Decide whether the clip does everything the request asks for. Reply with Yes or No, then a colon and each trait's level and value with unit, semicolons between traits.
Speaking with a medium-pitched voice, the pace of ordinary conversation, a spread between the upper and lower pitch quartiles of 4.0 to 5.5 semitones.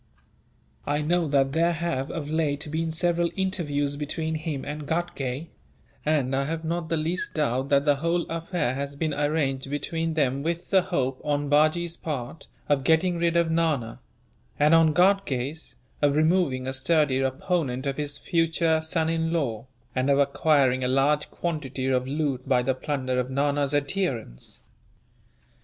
No: medium, 150 Hz; average, 160 wpm; average, 3.3 semitones